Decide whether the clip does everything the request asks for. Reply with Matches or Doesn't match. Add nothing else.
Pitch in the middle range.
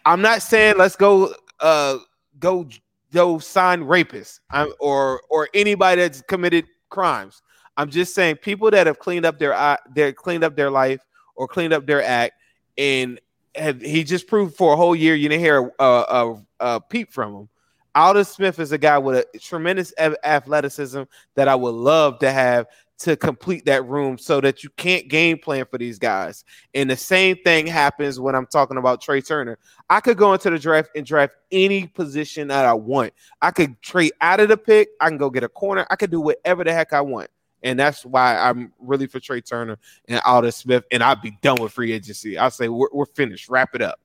Matches